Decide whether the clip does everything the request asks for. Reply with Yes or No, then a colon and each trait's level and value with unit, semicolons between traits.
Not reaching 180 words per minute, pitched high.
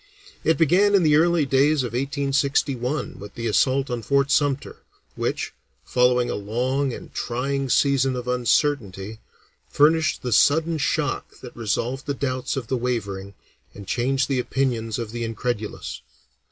No: average, 150 wpm; low, 130 Hz